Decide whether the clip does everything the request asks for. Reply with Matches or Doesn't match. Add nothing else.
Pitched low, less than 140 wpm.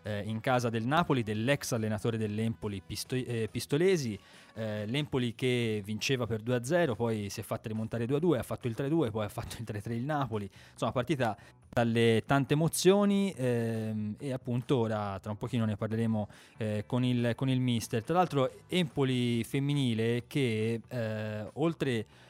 Doesn't match